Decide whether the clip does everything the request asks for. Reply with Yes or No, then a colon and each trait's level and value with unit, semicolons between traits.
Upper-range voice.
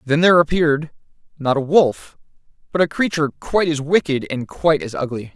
No: medium, 150 Hz